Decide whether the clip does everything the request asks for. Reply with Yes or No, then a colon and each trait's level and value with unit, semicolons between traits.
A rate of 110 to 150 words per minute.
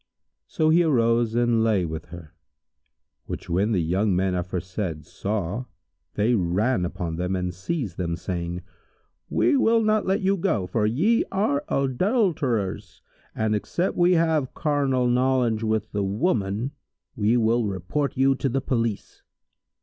Yes: average, 145 wpm